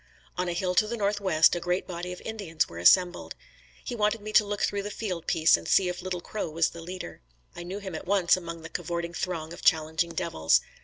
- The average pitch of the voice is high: No, medium, 180 Hz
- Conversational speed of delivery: No, fast, 235 wpm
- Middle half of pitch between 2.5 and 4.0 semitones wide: Yes, average, 3.0 semitones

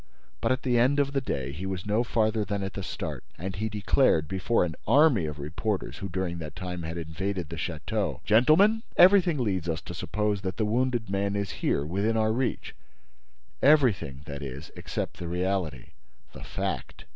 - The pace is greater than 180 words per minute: Yes, average, 190 wpm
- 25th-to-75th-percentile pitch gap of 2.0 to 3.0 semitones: No, wide, 5.5 semitones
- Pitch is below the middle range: Yes, low, 100 Hz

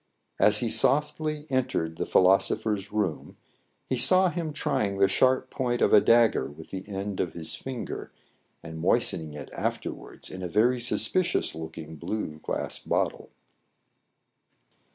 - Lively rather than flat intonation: Yes, wide, 7.3 semitones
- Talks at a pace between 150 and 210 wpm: No, average, 140 wpm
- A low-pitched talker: Yes, low, 105 Hz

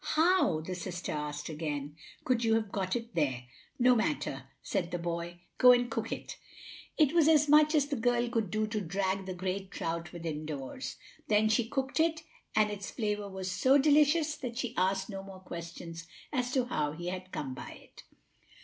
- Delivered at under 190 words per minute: No, average, 195 wpm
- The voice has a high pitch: Yes, high, 195 Hz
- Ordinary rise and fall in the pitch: No, wide, 6.4 semitones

